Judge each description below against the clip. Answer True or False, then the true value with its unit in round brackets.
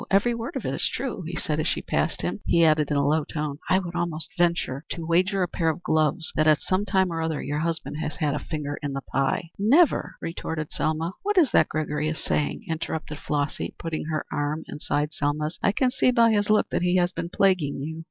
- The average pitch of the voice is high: False (160 Hz)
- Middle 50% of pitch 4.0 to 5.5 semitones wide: False (3.5 semitones)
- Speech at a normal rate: False (240 wpm)